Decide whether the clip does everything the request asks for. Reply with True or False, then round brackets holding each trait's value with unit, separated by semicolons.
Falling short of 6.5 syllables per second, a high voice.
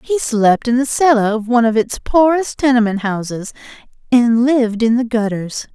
True (5.0 syllables/s; 235 Hz)